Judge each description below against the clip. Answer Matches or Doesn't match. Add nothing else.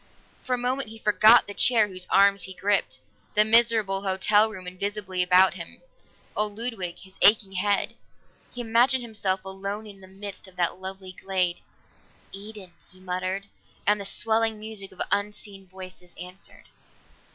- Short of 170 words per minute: Matches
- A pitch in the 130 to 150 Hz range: Doesn't match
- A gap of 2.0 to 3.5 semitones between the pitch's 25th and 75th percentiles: Matches